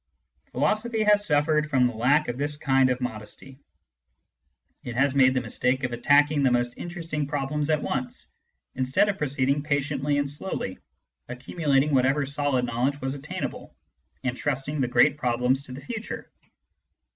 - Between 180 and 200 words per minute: No, average, 150 wpm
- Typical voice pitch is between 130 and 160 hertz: Yes, medium, 140 Hz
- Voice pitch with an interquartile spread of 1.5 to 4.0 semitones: Yes, narrow, 2.6 semitones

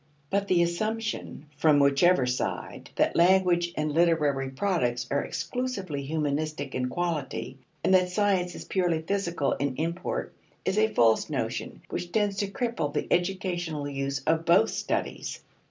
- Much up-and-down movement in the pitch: No, average, 4.9 semitones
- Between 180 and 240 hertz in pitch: No, medium, 170 Hz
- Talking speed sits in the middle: Yes, average, 145 wpm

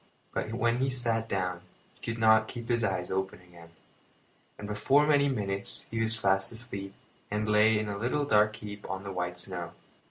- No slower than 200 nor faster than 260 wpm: No, average, 185 wpm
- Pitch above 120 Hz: No, low, 105 Hz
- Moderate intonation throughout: Yes, average, 3.0 semitones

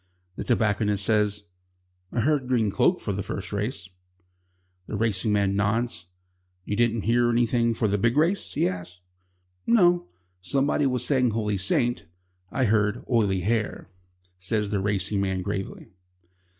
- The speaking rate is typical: Yes, average, 145 wpm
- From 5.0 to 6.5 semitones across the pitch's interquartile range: No, average, 3.3 semitones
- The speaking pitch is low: Yes, low, 110 Hz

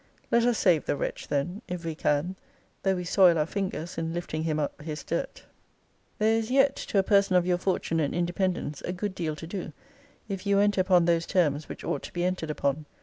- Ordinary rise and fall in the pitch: Yes, average, 3.4 semitones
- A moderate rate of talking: No, fast, 220 wpm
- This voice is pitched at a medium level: Yes, medium, 175 Hz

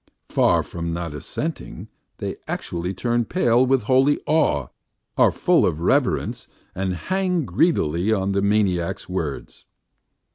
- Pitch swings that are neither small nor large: No, wide, 7.2 semitones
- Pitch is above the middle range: No, low, 100 Hz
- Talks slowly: Yes, slow, 130 wpm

